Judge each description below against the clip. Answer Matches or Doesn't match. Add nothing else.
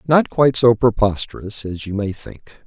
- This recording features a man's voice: Matches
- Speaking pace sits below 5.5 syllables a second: Matches